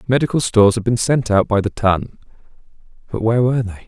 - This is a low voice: Yes, low, 115 Hz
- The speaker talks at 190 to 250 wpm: Yes, average, 200 wpm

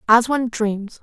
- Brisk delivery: No, average, 175 wpm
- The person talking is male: No, female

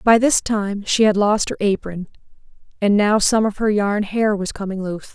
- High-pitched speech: Yes, high, 205 Hz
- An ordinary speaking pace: No, fast, 210 wpm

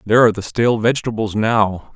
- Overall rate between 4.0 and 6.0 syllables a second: No, 6.6 syllables/s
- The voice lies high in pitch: No, low, 110 Hz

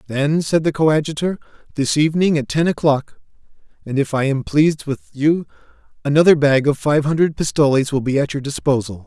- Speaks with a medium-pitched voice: Yes, medium, 145 Hz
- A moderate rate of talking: Yes, average, 180 wpm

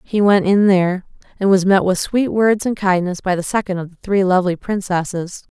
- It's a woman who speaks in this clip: Yes, female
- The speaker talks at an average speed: No, fast, 215 wpm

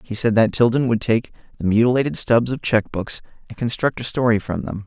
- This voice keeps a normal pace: No, fast, 220 wpm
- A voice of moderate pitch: No, low, 115 Hz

